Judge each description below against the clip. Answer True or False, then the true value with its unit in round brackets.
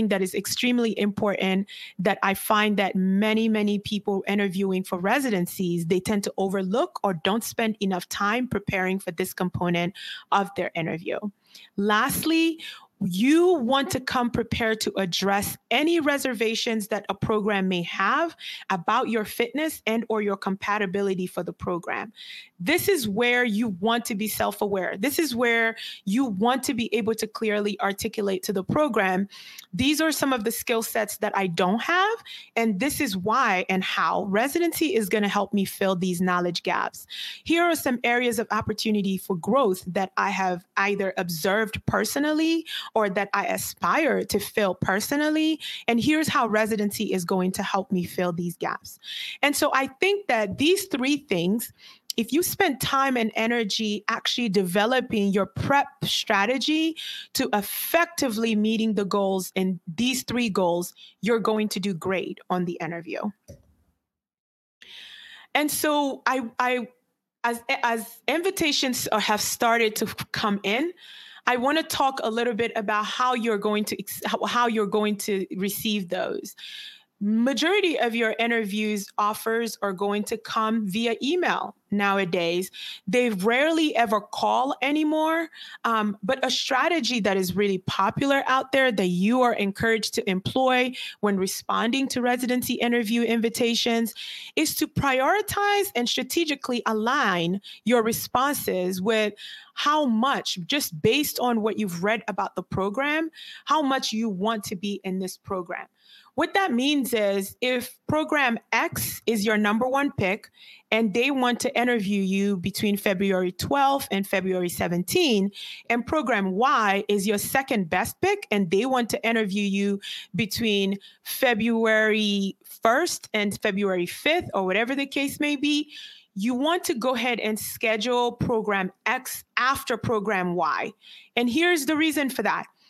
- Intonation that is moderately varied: True (4.7 semitones)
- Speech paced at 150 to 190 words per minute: True (155 wpm)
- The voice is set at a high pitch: True (225 Hz)